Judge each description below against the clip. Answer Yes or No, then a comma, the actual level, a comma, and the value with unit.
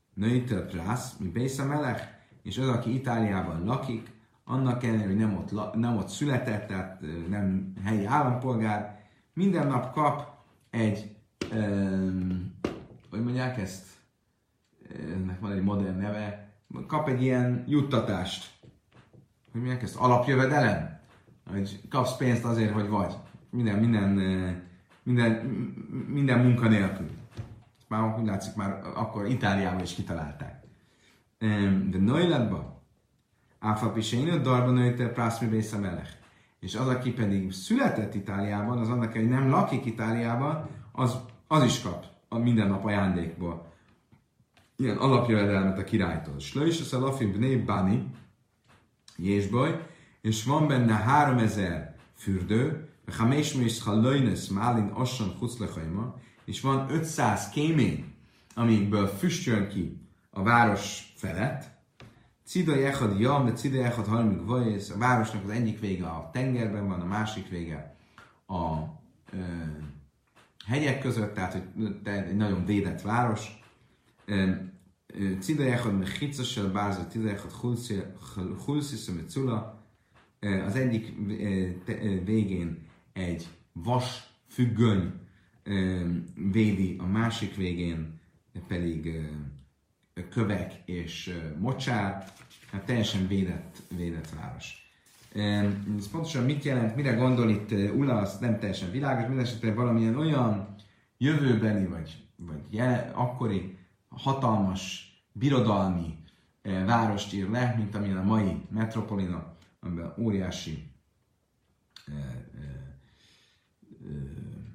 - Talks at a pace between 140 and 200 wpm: No, slow, 105 wpm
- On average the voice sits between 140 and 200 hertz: No, low, 105 Hz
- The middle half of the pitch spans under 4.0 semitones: No, average, 4.4 semitones